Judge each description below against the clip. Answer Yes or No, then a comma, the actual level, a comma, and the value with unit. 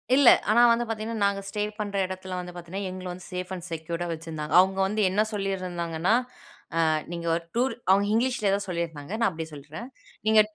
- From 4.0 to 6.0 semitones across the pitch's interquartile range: No, average, 3.6 semitones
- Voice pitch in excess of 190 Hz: No, medium, 185 Hz